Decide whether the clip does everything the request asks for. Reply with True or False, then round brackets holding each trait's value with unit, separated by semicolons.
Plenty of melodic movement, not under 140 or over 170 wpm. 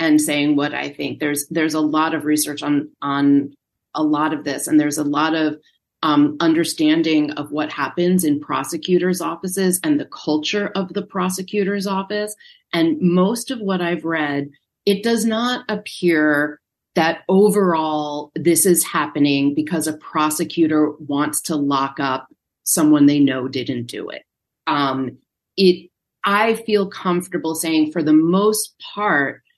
False (3.9 semitones; 150 wpm)